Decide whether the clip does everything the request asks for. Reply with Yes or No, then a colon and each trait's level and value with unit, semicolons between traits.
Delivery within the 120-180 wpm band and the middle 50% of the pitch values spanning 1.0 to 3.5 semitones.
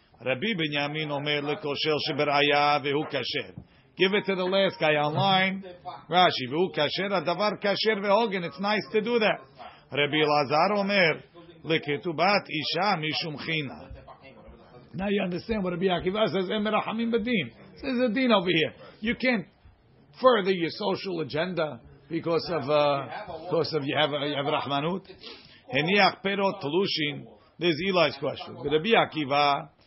No: average, 150 wpm; average, 4.8 semitones